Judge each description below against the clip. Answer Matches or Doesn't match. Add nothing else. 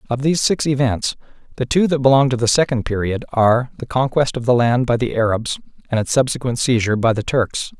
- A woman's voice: Doesn't match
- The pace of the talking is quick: Matches